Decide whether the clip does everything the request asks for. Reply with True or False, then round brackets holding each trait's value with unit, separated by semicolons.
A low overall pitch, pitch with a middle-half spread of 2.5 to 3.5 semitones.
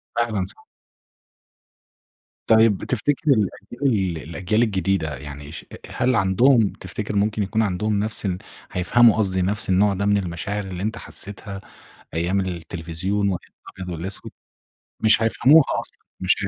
True (100 Hz; 3.1 semitones)